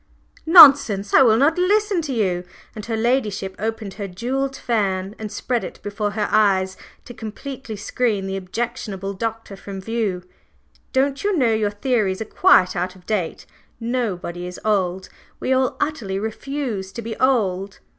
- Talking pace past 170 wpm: No, average, 160 wpm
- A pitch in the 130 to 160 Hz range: No, high, 220 Hz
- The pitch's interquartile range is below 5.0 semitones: Yes, average, 4.6 semitones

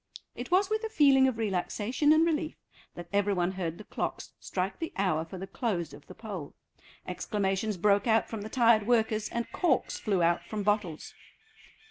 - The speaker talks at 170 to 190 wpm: Yes, average, 185 wpm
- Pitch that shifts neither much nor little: Yes, average, 4.6 semitones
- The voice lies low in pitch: No, high, 210 Hz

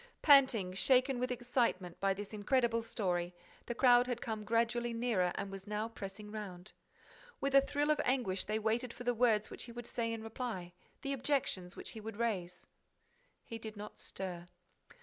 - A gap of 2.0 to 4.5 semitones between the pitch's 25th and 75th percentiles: Yes, average, 3.9 semitones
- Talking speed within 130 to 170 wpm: No, average, 180 wpm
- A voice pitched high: Yes, high, 225 Hz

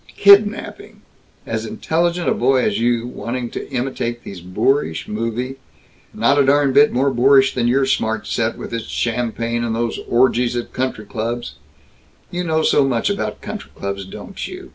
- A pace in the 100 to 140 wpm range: No, average, 175 wpm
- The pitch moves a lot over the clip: No, average, 3.0 semitones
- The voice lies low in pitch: Yes, low, 120 Hz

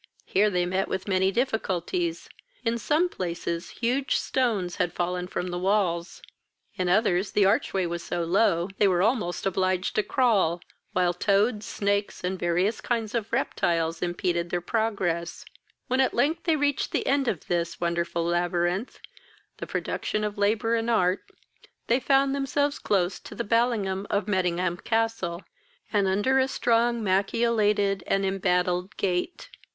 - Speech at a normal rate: Yes, average, 155 wpm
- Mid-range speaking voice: No, high, 195 Hz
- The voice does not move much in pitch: No, average, 4.3 semitones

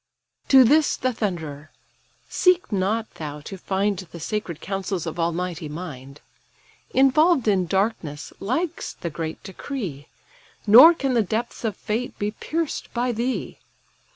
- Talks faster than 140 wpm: No, slow, 135 wpm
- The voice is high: Yes, high, 200 Hz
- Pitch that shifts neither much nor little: No, wide, 6.6 semitones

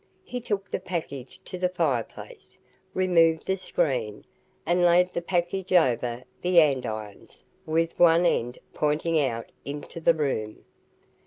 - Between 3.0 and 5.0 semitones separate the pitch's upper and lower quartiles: No, wide, 5.4 semitones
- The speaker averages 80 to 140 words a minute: Yes, slow, 135 wpm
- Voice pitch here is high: No, medium, 165 Hz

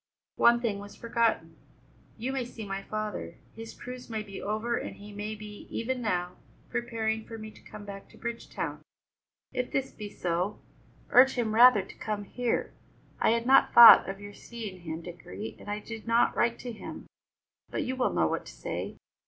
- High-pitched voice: Yes, high, 220 Hz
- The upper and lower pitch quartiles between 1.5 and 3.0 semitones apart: Yes, average, 2.7 semitones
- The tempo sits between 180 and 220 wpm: Yes, average, 190 wpm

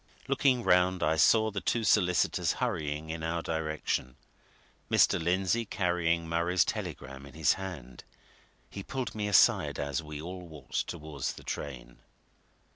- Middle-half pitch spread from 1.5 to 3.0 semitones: No, average, 3.8 semitones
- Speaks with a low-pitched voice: Yes, very low, 85 Hz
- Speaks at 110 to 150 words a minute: Yes, average, 140 wpm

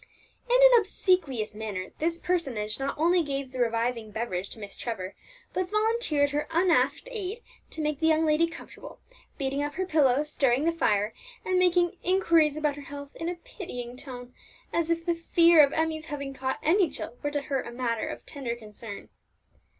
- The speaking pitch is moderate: No, very high, 295 Hz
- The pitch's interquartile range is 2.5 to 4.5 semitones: No, wide, 5.5 semitones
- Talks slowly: No, average, 185 wpm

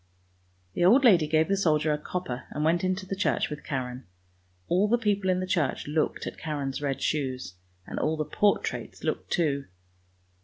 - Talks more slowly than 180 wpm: No, average, 185 wpm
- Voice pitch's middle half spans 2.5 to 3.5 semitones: No, average, 4.3 semitones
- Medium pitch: Yes, medium, 160 Hz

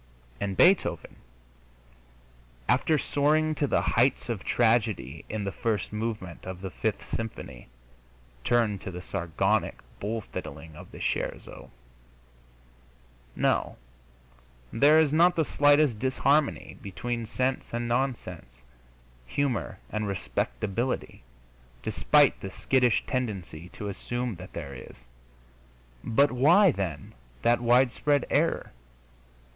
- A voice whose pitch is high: No, low, 115 Hz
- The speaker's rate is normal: No, slow, 110 wpm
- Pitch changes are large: Yes, wide, 5.7 semitones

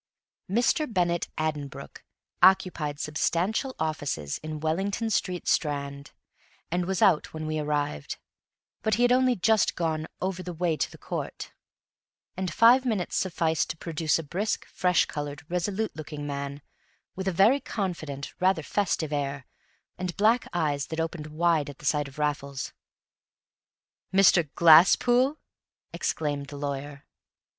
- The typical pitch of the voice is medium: Yes, medium, 160 Hz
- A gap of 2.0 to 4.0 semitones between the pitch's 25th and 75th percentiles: No, average, 4.5 semitones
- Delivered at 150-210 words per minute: No, average, 140 wpm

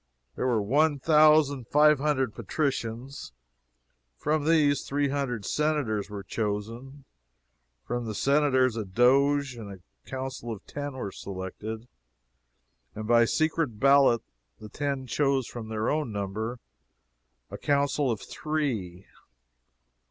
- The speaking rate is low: Yes, slow, 120 wpm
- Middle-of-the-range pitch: No, low, 130 Hz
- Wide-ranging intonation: No, average, 4.6 semitones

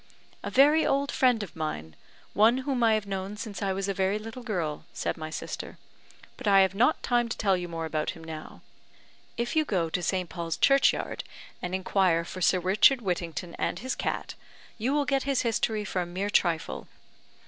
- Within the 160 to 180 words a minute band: No, average, 200 wpm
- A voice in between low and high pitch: No, high, 195 Hz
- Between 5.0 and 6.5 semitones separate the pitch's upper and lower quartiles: Yes, average, 5.3 semitones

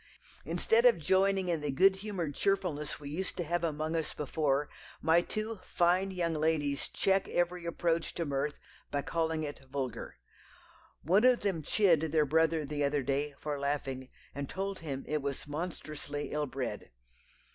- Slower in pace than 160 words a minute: No, average, 165 wpm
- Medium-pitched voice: Yes, medium, 160 Hz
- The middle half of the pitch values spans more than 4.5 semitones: No, average, 3.8 semitones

